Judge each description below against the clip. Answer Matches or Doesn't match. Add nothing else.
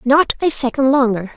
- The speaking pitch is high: Matches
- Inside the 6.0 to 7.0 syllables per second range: Doesn't match